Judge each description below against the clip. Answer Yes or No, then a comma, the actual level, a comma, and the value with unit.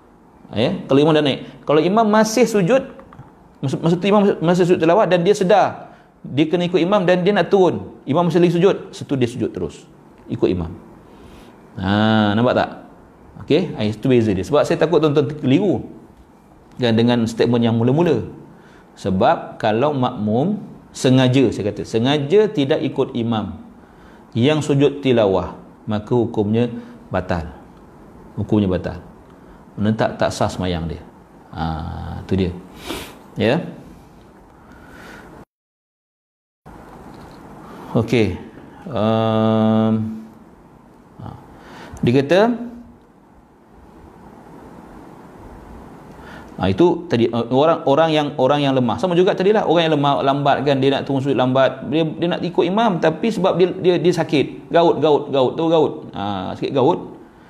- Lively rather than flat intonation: Yes, wide, 7.9 semitones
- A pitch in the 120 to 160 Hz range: Yes, low, 135 Hz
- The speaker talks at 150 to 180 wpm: No, average, 135 wpm